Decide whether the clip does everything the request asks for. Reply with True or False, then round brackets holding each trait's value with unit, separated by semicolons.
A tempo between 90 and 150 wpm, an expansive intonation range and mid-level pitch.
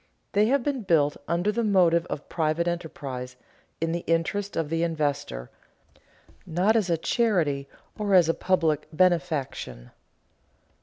False (140 wpm; 3.7 semitones; 170 Hz)